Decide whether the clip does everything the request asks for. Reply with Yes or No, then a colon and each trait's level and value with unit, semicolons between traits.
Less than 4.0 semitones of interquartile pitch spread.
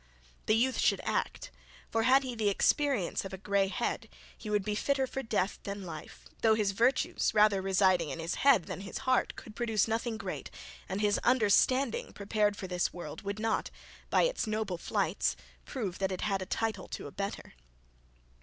Yes: average, 3.1 semitones